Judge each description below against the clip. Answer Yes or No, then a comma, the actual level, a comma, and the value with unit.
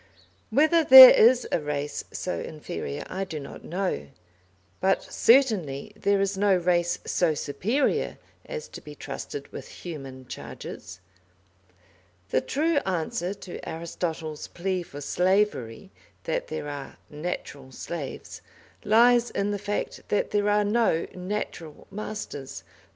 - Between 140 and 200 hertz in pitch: Yes, medium, 185 Hz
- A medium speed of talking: No, slow, 130 wpm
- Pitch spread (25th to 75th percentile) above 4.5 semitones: Yes, wide, 5.6 semitones